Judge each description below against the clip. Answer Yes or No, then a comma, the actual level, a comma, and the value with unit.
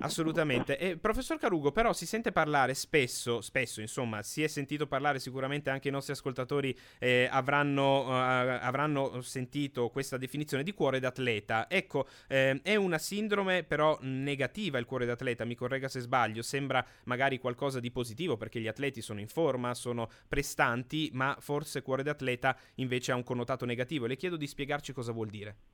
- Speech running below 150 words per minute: No, fast, 170 wpm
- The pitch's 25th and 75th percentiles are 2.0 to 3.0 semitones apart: Yes, narrow, 2.6 semitones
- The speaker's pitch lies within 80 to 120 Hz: No, low, 135 Hz